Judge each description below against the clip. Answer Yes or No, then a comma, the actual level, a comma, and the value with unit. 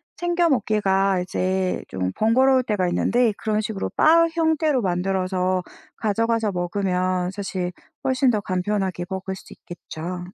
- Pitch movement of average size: Yes, average, 4.1 semitones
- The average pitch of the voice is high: Yes, high, 195 Hz